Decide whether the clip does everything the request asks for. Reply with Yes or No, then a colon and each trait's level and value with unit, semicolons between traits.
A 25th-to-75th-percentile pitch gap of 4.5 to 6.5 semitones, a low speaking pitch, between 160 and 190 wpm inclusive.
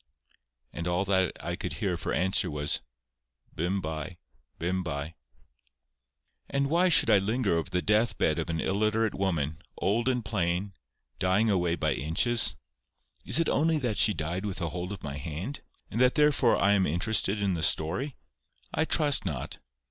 Yes: average, 5.1 semitones; very low, 95 Hz; average, 170 wpm